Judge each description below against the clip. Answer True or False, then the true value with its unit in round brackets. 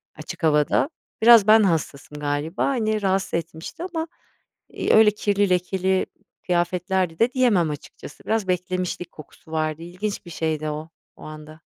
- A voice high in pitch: False (180 Hz)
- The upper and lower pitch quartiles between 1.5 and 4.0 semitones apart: False (4.8 semitones)